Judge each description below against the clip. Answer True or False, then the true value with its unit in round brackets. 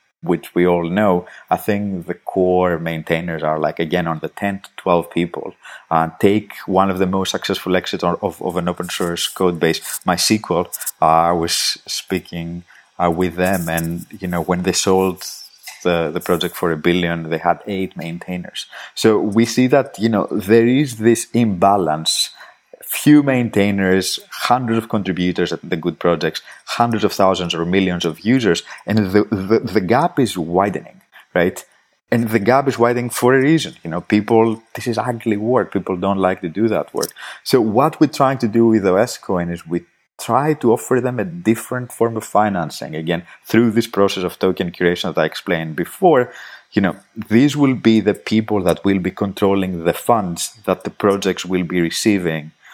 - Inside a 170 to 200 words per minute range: True (185 wpm)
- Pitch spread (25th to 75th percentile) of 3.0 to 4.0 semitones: False (4.5 semitones)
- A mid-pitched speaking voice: False (95 Hz)